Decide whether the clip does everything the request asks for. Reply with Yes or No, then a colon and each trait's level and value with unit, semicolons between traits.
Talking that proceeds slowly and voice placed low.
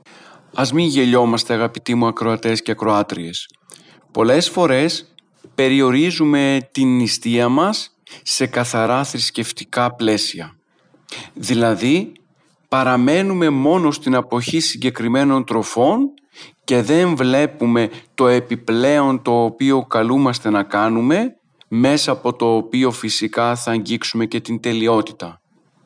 Yes: slow, 105 wpm; low, 125 Hz